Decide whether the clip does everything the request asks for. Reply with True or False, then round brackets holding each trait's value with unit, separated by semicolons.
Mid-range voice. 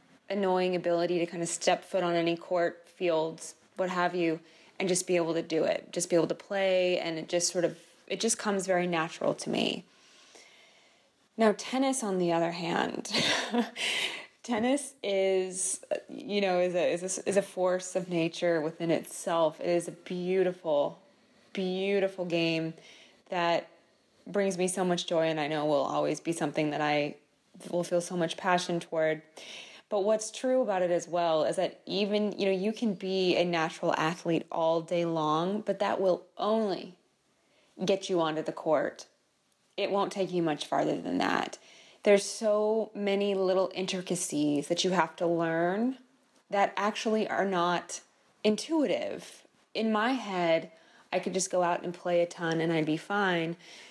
True (180 Hz)